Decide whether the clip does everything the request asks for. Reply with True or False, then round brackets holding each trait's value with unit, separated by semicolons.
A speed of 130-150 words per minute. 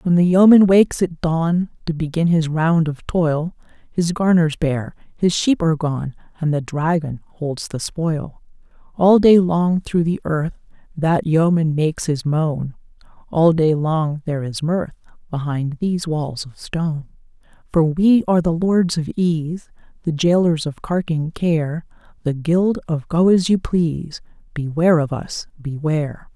False (160 wpm)